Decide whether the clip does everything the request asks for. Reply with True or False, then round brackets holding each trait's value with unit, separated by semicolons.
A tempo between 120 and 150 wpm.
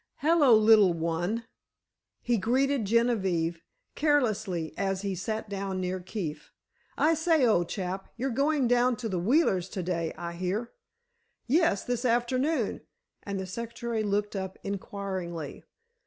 True (135 wpm)